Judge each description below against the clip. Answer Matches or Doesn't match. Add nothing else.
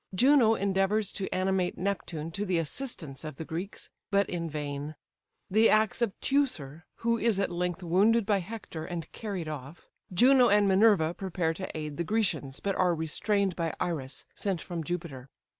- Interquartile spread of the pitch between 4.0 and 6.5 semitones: Matches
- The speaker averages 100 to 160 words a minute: Doesn't match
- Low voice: Doesn't match